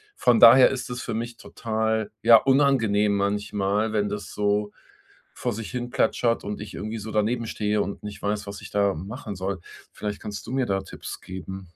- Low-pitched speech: Yes, low, 105 Hz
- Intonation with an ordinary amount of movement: No, narrow, 2.2 semitones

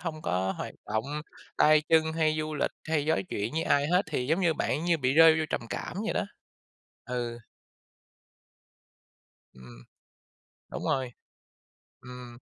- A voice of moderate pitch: Yes, medium, 150 Hz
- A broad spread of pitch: No, average, 4.7 semitones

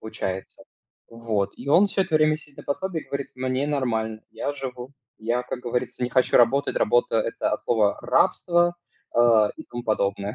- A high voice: No, low, 125 Hz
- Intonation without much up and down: No, average, 4.1 semitones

